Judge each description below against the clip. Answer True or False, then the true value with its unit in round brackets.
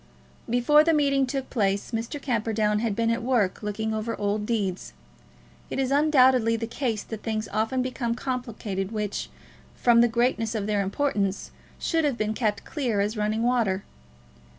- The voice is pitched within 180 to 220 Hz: False (230 Hz)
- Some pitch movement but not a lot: True (3.2 semitones)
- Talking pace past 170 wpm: False (165 wpm)